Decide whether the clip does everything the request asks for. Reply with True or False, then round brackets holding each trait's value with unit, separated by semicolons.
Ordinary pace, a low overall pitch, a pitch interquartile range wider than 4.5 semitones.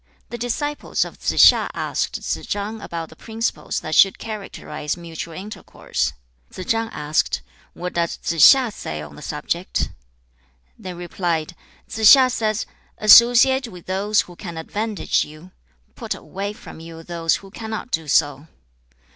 False (150 wpm; 185 Hz; 5.1 semitones)